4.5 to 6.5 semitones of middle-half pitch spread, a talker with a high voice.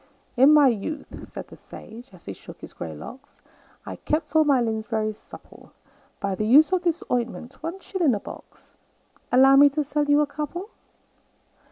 Yes: average, 5.2 semitones; very high, 275 Hz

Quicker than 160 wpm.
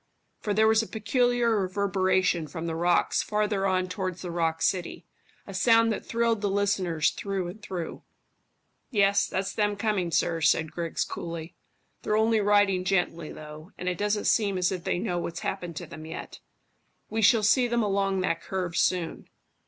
Yes: average, 175 wpm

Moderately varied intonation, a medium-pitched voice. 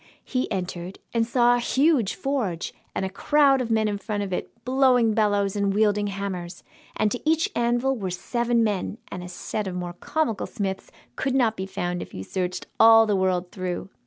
No: average, 4.2 semitones; high, 210 Hz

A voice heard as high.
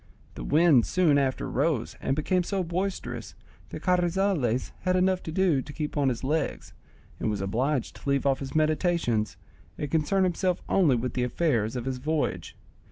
No: medium, 150 Hz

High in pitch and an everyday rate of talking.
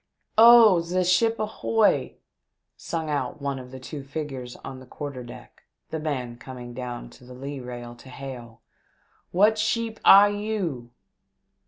No: medium, 140 Hz; average, 165 wpm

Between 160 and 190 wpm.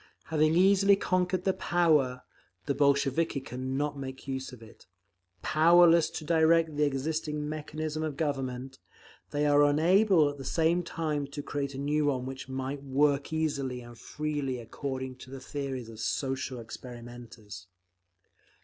No: average, 150 wpm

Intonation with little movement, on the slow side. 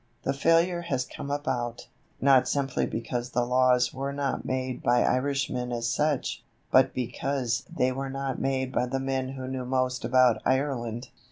No: narrow, 1.6 semitones; average, 165 wpm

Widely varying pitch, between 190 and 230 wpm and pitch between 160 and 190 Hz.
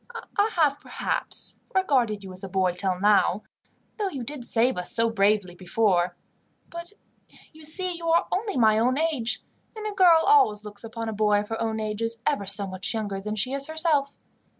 No: wide, 7.3 semitones; average, 195 wpm; high, 225 Hz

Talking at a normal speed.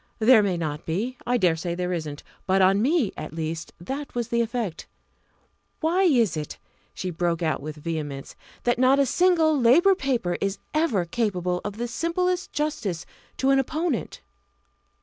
Yes: average, 170 wpm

